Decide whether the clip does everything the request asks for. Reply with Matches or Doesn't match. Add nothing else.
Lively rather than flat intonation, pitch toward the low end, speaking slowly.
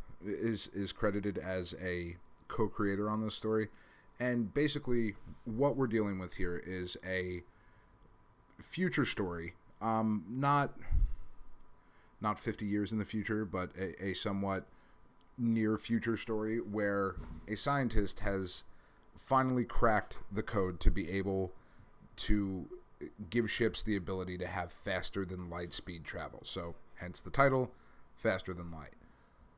Doesn't match